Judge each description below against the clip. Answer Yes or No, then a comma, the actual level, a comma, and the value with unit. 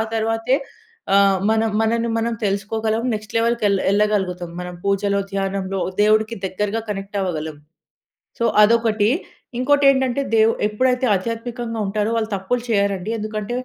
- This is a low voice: No, high, 215 Hz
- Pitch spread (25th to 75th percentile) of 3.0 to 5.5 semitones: No, narrow, 2.5 semitones